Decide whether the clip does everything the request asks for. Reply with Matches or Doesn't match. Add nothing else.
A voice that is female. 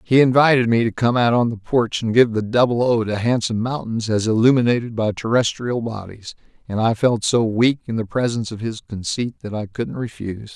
Doesn't match